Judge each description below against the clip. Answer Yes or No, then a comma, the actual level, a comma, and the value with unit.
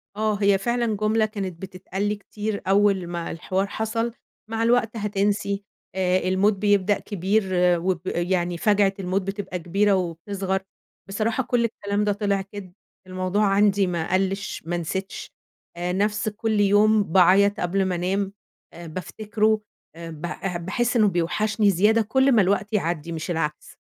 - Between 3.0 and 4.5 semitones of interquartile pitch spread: No, narrow, 2.5 semitones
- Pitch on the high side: Yes, high, 195 Hz